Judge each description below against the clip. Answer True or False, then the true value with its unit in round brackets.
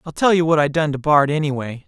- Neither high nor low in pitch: True (150 Hz)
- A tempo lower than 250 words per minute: False (290 wpm)